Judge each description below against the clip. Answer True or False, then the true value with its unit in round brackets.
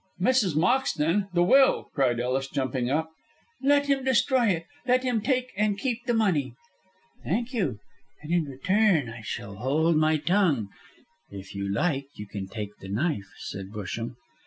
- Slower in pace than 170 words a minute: True (160 wpm)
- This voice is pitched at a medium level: True (160 Hz)